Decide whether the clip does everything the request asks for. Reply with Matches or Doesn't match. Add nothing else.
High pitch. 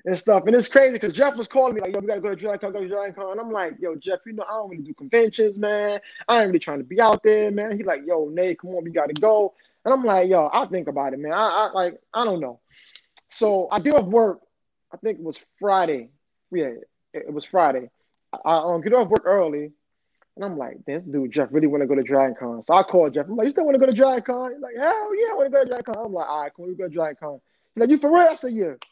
Matches